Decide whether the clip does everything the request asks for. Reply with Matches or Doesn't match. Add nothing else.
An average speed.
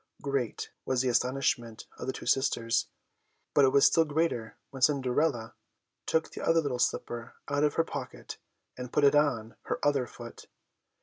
Matches